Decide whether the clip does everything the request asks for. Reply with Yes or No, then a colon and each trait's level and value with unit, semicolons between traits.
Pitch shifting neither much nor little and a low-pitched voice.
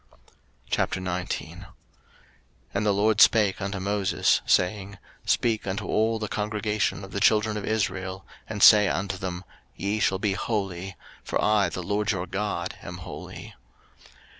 No: narrow, 1.9 semitones; low, 100 Hz